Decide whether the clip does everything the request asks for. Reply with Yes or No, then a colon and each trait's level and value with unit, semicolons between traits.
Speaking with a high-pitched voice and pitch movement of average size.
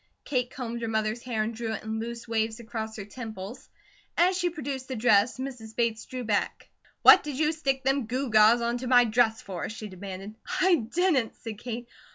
Yes: high, 235 Hz; average, 3.0 semitones